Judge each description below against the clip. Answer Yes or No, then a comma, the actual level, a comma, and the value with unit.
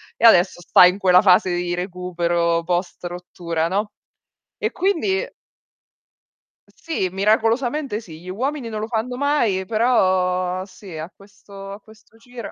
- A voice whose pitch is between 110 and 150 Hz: No, high, 195 Hz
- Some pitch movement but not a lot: Yes, average, 4.1 semitones